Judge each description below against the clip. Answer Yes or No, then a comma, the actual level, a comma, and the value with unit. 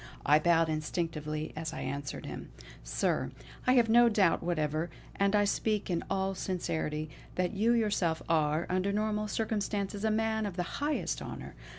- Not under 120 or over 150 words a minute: No, average, 165 wpm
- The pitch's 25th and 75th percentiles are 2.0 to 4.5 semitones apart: No, average, 5.1 semitones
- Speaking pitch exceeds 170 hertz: Yes, medium, 185 Hz